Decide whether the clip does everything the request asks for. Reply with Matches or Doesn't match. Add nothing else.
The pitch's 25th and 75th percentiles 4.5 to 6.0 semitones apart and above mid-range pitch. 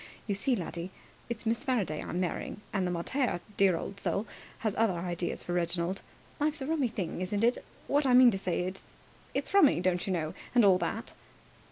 Matches